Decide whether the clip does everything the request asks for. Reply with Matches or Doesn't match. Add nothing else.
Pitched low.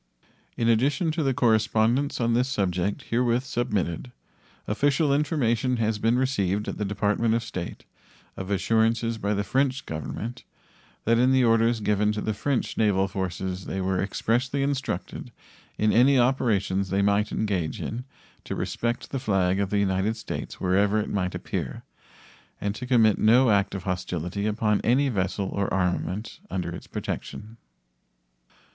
Matches